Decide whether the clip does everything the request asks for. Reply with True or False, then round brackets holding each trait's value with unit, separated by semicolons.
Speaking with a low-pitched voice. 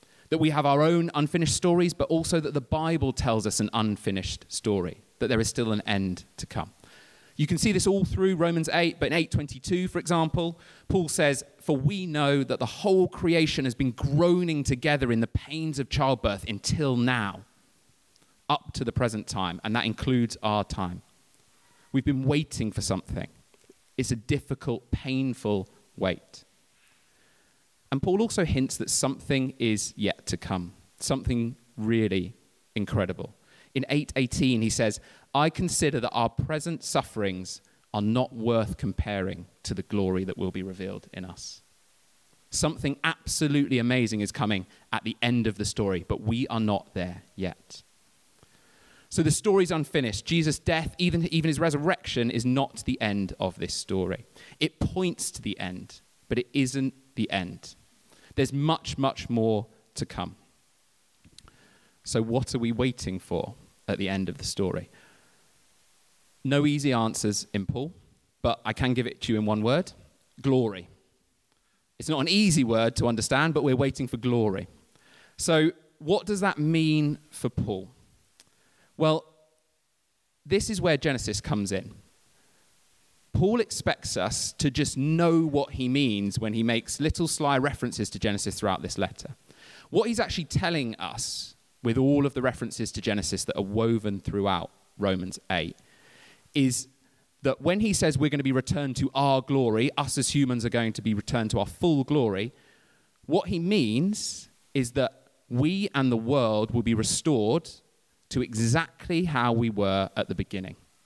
True (130 Hz)